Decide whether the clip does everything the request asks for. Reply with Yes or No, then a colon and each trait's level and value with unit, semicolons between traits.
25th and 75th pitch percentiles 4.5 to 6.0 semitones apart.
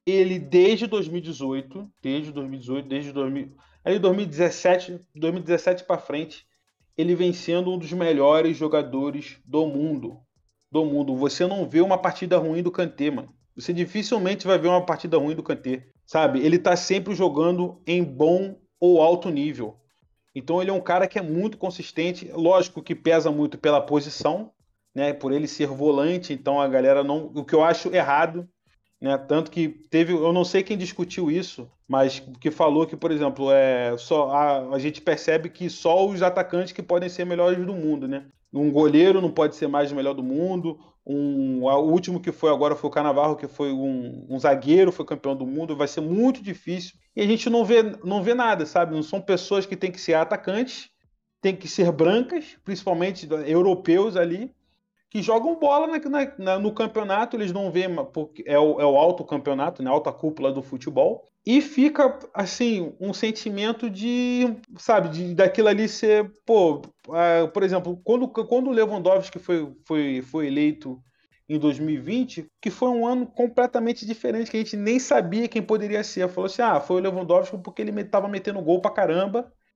Yes: average, 4.8 semitones